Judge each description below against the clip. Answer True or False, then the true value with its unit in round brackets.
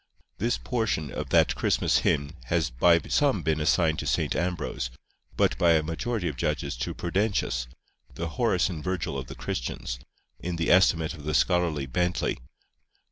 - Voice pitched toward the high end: False (85 Hz)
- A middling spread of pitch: True (3.1 semitones)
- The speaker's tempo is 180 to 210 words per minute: False (165 wpm)